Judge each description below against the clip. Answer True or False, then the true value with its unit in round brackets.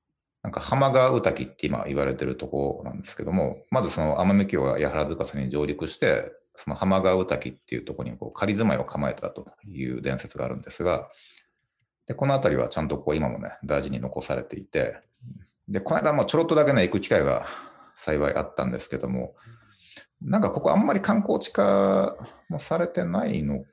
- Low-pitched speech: True (95 Hz)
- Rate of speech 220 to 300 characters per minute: False (385 characters per minute)